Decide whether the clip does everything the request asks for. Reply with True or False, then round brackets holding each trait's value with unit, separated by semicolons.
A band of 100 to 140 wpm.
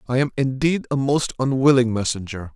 False (165 wpm)